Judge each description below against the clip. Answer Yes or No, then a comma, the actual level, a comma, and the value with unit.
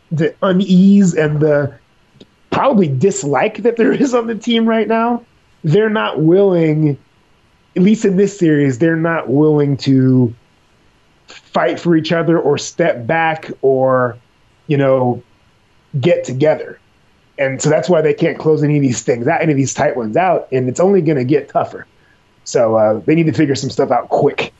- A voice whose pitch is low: No, medium, 155 Hz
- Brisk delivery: No, average, 180 wpm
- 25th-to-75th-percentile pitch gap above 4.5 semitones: Yes, average, 5.2 semitones